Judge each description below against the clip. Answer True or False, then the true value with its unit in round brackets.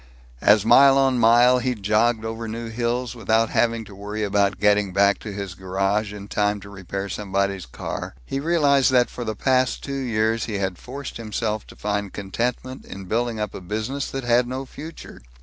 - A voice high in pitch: False (110 Hz)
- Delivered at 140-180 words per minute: False (190 wpm)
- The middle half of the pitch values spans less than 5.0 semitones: True (3.5 semitones)